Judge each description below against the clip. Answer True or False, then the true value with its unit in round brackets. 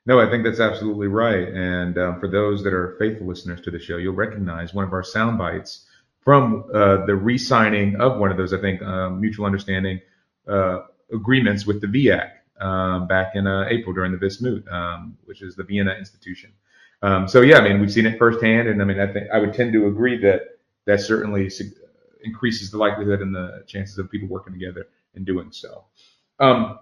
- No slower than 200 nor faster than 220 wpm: True (205 wpm)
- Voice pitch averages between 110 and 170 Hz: False (100 Hz)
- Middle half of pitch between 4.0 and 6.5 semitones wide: False (2.7 semitones)